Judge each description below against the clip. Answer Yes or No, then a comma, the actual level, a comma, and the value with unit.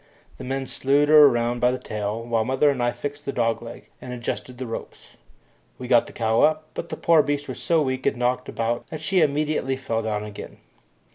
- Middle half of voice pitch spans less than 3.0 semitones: No, average, 3.7 semitones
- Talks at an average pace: No, fast, 220 wpm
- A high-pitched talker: No, low, 130 Hz